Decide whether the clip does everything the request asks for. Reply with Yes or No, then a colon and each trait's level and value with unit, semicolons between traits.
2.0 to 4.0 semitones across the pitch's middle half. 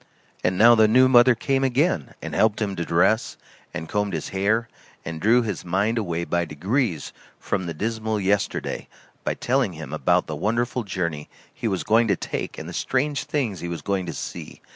No: average, 5.3 semitones